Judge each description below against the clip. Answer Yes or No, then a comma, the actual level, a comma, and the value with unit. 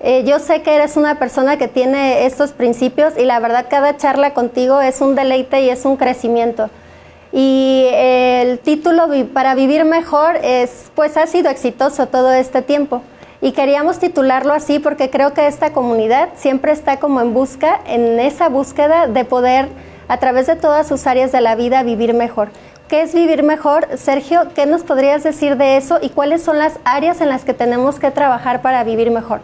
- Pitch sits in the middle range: No, very high, 275 Hz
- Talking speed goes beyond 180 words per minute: Yes, fast, 190 wpm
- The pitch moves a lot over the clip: No, narrow, 2.6 semitones